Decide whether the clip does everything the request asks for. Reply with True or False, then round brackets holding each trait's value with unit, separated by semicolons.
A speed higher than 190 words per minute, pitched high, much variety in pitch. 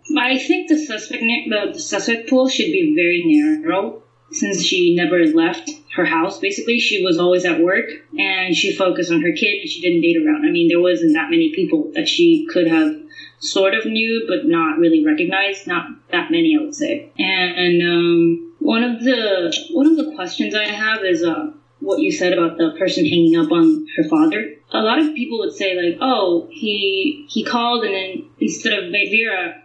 True (200 wpm; 300 Hz; 8.6 semitones)